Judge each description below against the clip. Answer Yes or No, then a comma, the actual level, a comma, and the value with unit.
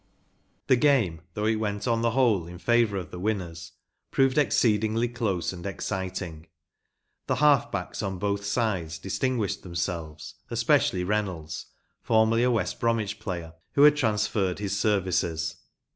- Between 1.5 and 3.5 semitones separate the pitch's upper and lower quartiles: No, average, 4.4 semitones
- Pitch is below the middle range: Yes, low, 100 Hz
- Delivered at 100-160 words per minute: Yes, average, 150 wpm